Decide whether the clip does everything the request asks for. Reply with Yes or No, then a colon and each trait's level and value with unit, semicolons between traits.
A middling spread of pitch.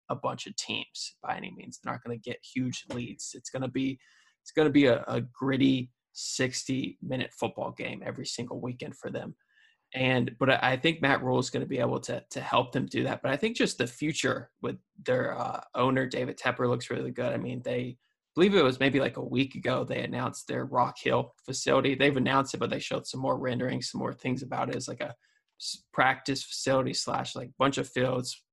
No: narrow, 1.3 semitones